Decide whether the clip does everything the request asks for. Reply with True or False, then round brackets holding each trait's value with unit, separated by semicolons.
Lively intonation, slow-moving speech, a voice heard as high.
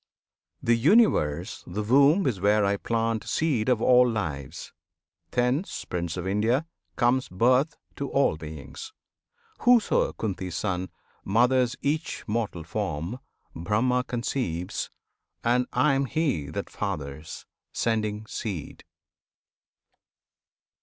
False (6.0 semitones; 110 wpm; 115 Hz)